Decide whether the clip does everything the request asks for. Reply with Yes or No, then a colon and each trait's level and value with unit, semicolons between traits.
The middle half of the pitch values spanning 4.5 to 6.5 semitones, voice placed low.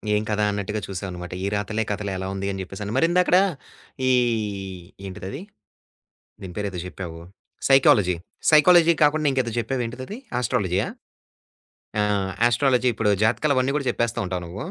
Yes: wide, 5.5 semitones; low, 110 Hz